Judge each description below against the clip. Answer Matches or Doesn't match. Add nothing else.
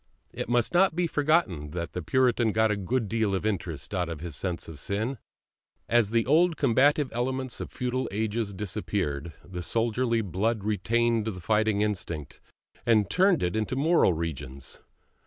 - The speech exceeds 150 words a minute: Matches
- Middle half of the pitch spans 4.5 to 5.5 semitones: Matches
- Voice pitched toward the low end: Matches